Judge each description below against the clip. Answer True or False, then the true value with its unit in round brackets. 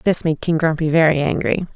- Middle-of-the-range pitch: True (160 Hz)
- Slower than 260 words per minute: True (205 wpm)